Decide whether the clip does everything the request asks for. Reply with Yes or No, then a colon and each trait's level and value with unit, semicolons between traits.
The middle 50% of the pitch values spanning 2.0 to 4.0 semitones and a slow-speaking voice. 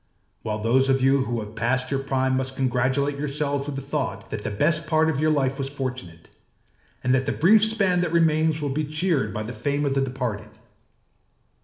No: average, 3.0 semitones; fast, 205 wpm